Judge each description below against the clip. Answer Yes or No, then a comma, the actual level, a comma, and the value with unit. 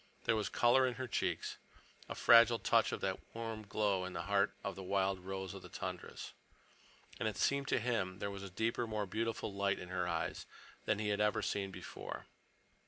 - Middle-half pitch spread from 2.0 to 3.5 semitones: Yes, average, 2.9 semitones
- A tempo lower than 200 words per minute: No, fast, 205 wpm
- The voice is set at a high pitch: No, low, 100 Hz